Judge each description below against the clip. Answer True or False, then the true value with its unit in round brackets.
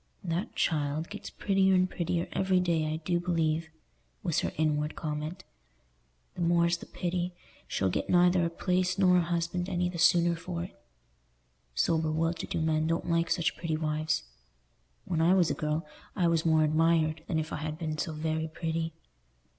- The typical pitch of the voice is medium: True (165 Hz)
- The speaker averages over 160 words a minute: True (180 wpm)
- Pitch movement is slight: True (2.0 semitones)